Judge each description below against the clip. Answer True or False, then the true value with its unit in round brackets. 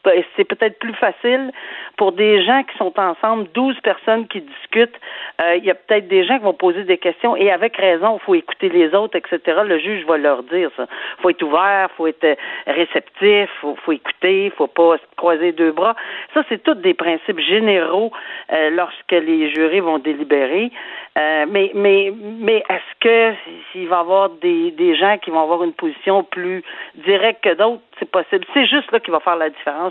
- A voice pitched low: False (195 Hz)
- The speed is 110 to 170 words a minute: False (210 wpm)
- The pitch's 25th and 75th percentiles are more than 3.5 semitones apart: True (5.0 semitones)